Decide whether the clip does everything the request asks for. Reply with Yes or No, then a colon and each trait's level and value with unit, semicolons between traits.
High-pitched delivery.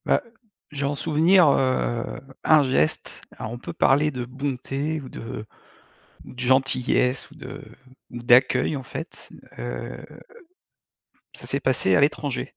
No: low, 135 Hz